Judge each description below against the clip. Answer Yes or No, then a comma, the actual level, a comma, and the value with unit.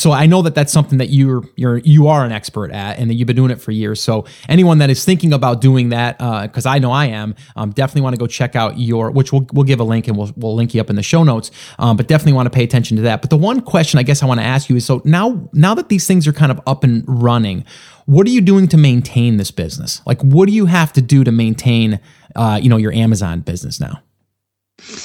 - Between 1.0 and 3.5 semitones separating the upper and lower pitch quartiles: No, average, 4.7 semitones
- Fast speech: Yes, fast, 280 wpm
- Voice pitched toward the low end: Yes, low, 130 Hz